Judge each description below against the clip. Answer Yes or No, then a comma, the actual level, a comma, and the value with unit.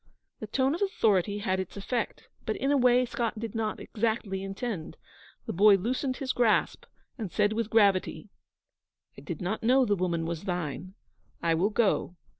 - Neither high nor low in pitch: No, high, 215 Hz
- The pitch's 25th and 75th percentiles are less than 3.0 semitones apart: No, average, 4.0 semitones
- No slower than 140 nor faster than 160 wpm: No, average, 175 wpm